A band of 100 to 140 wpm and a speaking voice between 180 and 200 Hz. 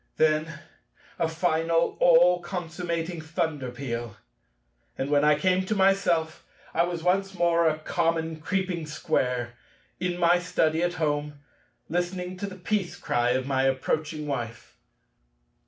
No: slow, 135 wpm; medium, 165 Hz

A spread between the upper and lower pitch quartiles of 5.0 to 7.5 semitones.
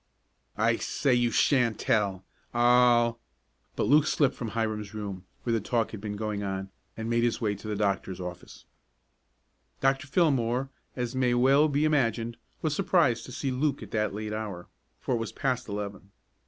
No: average, 3.8 semitones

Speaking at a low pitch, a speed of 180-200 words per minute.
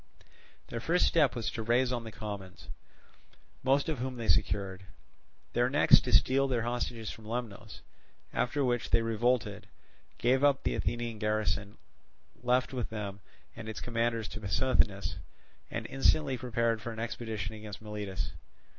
No: low, 115 Hz; average, 150 wpm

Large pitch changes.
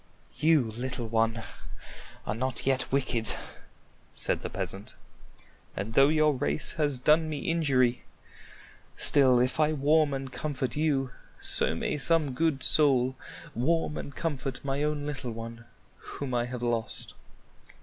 No: average, 3.7 semitones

